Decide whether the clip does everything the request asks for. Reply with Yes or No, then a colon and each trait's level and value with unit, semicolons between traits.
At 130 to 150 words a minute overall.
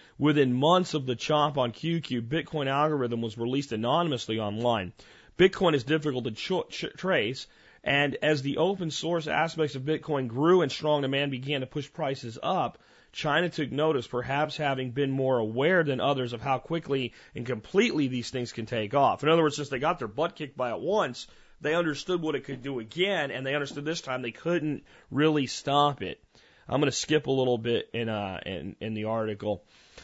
No: average, 200 wpm